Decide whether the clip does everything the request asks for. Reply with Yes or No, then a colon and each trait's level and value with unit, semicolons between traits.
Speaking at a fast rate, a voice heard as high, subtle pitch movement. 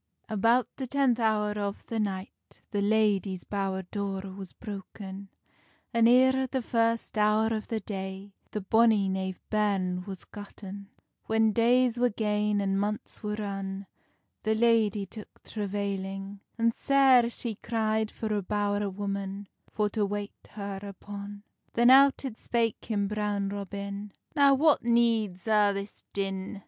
No: average, 145 wpm; high, 210 Hz; narrow, 2.3 semitones